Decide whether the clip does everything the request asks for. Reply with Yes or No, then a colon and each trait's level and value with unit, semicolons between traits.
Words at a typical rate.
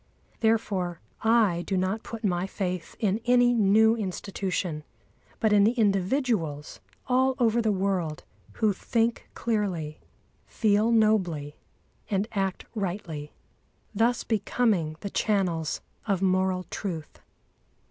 No: slow, 115 wpm